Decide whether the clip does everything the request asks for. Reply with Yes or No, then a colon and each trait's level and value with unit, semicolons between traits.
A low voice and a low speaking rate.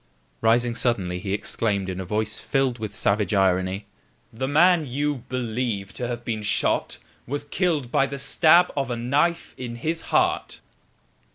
No: low, 120 Hz; average, 160 wpm